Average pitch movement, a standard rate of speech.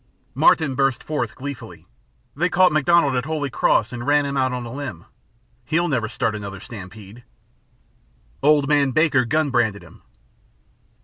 Yes: average, 3.8 semitones; average, 150 wpm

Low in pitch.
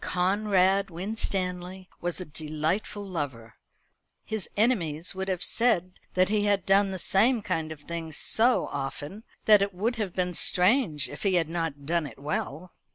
No: medium, 185 Hz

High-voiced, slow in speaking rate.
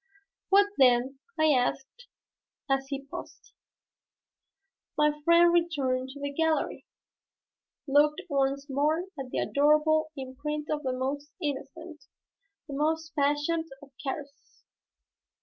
Yes: very high, 290 Hz; slow, 115 wpm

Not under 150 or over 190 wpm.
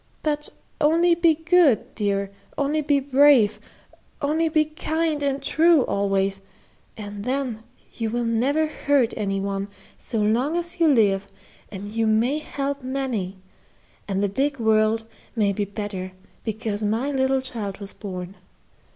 No: average, 140 wpm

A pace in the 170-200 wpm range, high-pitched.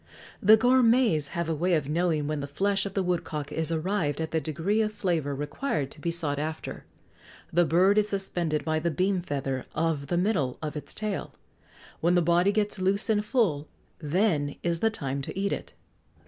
No: average, 195 wpm; medium, 170 Hz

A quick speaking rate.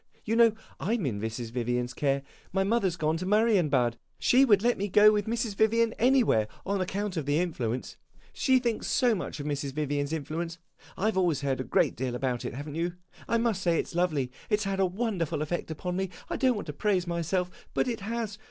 Yes: fast, 230 wpm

